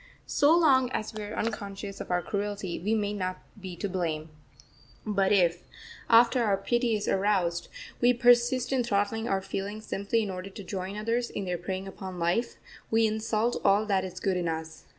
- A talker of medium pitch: No, high, 205 Hz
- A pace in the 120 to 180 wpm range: No, average, 190 wpm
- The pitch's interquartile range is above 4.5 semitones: No, average, 3.2 semitones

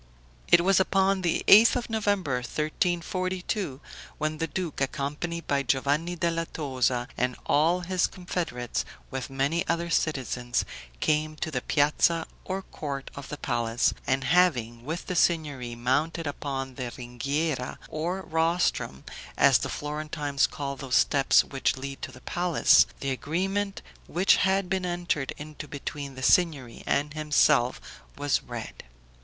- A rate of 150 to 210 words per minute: No, average, 140 wpm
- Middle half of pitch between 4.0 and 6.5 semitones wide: Yes, average, 4.5 semitones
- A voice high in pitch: No, medium, 150 Hz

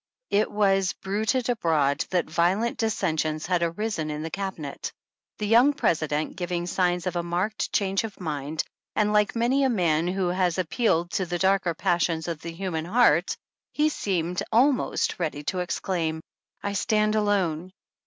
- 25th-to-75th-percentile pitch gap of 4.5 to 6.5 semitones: No, average, 4.1 semitones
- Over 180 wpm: No, average, 160 wpm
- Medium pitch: Yes, medium, 180 Hz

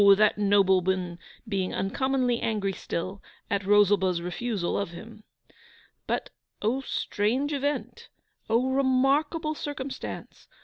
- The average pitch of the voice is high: Yes, high, 215 Hz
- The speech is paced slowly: Yes, slow, 100 wpm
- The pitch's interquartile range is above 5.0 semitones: Yes, wide, 5.4 semitones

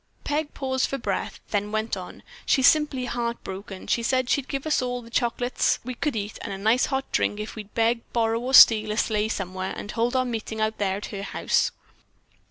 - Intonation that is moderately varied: Yes, average, 3.2 semitones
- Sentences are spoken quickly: Yes, fast, 215 wpm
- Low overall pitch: No, high, 230 Hz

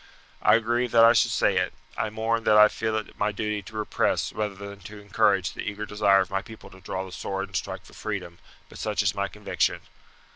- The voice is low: Yes, low, 105 Hz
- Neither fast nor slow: No, fast, 230 wpm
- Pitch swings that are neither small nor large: No, narrow, 1.8 semitones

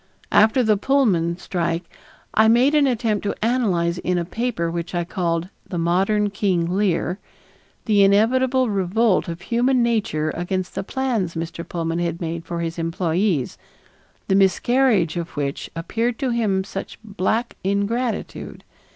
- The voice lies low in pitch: No, high, 195 Hz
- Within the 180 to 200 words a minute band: No, average, 145 wpm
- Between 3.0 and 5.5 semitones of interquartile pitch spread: Yes, average, 5.1 semitones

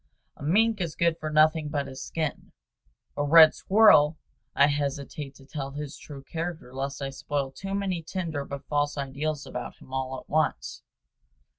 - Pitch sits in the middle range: Yes, medium, 145 Hz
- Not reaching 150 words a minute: No, average, 170 wpm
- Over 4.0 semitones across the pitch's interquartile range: No, average, 2.7 semitones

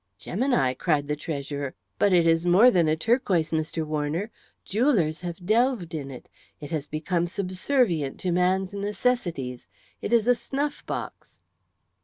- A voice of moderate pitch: Yes, medium, 175 Hz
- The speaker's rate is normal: Yes, average, 150 wpm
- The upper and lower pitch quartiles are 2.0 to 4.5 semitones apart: No, average, 5.3 semitones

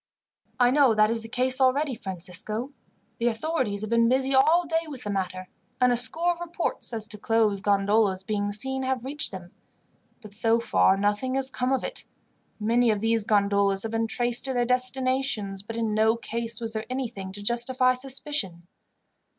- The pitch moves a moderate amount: Yes, average, 3.9 semitones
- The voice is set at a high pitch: Yes, high, 230 Hz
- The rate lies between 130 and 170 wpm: No, average, 185 wpm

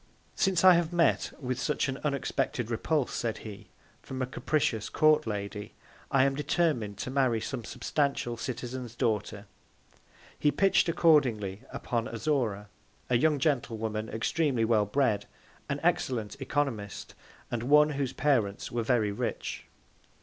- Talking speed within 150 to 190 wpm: No, slow, 135 wpm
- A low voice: Yes, low, 125 Hz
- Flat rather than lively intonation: No, average, 4.8 semitones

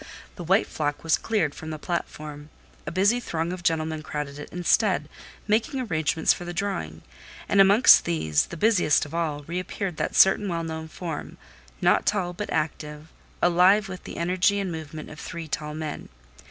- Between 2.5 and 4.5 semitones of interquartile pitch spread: Yes, average, 3.8 semitones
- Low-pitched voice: No, medium, 165 Hz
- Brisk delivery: No, average, 170 wpm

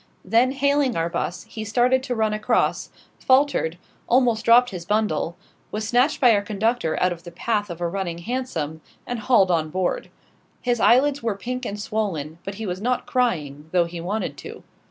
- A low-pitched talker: No, high, 215 Hz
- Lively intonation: Yes, wide, 5.9 semitones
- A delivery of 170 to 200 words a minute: Yes, average, 185 wpm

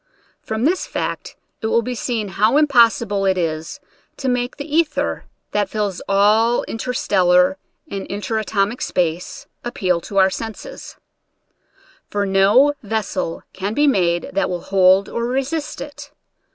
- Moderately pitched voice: No, high, 210 Hz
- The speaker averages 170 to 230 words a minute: No, average, 145 wpm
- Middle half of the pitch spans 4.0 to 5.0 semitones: Yes, average, 4.5 semitones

